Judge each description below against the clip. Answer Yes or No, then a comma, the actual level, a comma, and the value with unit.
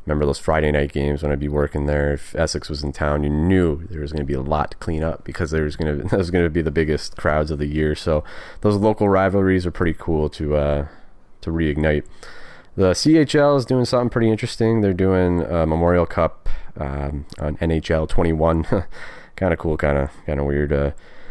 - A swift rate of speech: Yes, fast, 225 wpm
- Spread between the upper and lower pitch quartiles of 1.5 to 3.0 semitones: No, average, 3.5 semitones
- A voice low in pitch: Yes, very low, 80 Hz